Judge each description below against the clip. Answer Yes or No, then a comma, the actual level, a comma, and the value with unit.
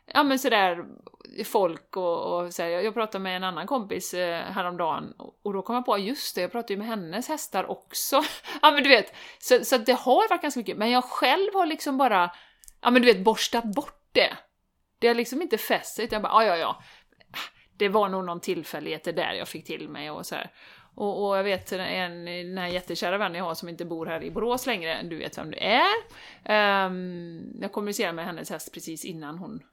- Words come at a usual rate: No, fast, 215 wpm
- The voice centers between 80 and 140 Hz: No, high, 205 Hz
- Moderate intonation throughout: No, wide, 6.1 semitones